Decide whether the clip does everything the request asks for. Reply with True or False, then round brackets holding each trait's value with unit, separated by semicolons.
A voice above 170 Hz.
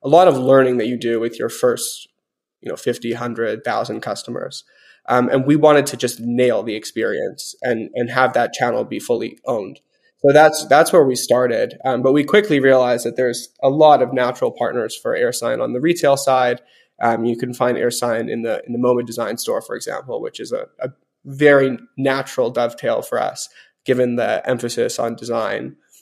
False (135 Hz)